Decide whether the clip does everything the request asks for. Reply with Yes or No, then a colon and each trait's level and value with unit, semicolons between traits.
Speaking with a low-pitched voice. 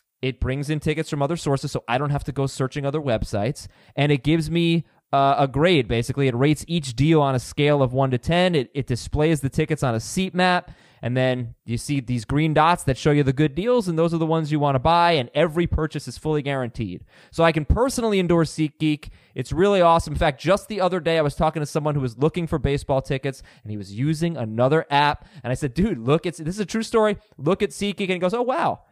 No: medium, 150 Hz